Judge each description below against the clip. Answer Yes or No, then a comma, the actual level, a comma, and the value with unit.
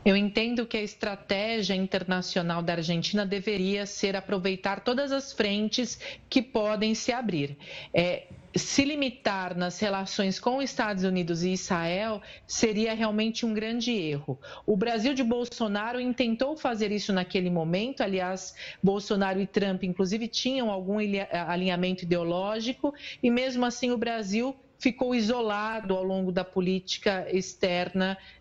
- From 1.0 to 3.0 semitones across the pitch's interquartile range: No, average, 3.9 semitones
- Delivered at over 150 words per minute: No, average, 135 wpm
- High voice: Yes, high, 205 Hz